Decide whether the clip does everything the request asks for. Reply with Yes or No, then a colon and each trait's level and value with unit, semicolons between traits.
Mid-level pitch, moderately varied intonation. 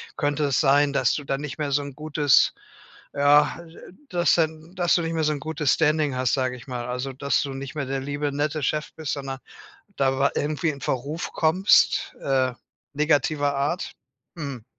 No: medium, 145 Hz; narrow, 2.2 semitones